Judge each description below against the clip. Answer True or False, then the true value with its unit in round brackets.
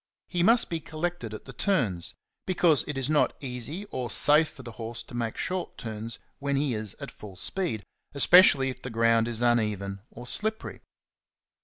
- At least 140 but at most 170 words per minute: False (180 wpm)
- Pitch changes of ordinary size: False (5.9 semitones)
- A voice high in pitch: False (125 Hz)